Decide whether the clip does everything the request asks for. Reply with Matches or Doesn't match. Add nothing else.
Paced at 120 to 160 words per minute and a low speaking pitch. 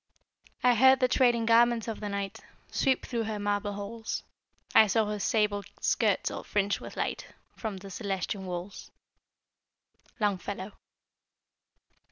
Doesn't match